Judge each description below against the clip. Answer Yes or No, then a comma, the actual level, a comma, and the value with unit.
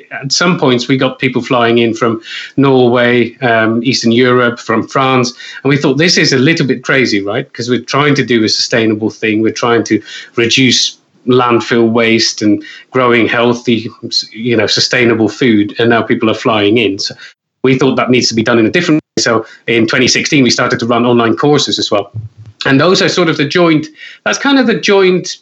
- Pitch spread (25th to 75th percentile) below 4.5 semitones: Yes, average, 2.9 semitones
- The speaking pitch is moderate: No, low, 120 Hz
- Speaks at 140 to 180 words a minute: No, fast, 205 wpm